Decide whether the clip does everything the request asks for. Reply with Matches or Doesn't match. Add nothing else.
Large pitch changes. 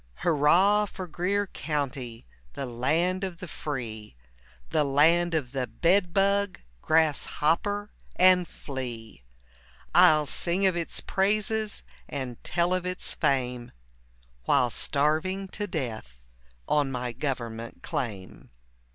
Matches